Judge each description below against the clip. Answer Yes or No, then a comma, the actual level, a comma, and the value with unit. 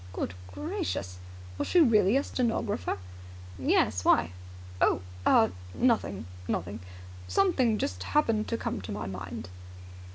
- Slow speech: Yes, slow, 125 wpm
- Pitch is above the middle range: No, low, 110 Hz